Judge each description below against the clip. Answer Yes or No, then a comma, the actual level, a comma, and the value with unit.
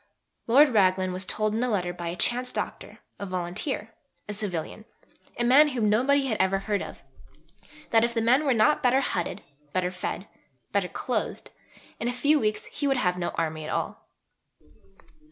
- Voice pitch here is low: No, high, 215 Hz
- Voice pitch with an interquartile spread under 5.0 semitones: No, average, 5.3 semitones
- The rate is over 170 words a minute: Yes, average, 180 wpm